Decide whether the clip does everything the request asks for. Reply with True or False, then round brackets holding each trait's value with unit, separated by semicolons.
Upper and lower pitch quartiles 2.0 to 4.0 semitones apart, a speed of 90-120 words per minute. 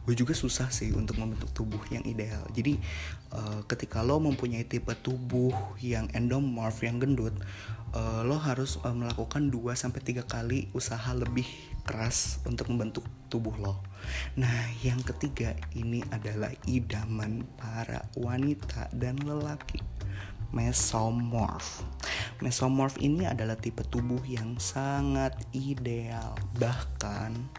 True (2.8 semitones; 110 wpm)